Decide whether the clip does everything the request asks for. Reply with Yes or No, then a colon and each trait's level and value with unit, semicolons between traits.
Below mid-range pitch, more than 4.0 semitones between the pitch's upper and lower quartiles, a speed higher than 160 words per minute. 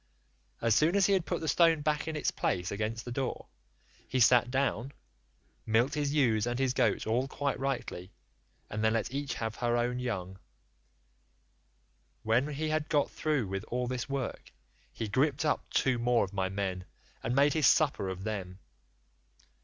Yes: low, 125 Hz; average, 4.6 semitones; average, 180 wpm